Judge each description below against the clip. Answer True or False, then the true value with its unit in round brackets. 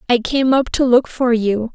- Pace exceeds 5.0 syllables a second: False (4.5 syllables/s)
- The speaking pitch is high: True (245 Hz)